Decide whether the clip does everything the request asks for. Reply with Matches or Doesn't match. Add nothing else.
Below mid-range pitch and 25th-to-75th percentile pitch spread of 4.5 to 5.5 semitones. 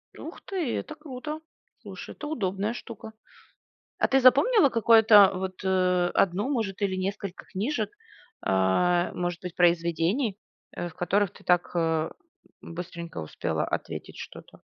Doesn't match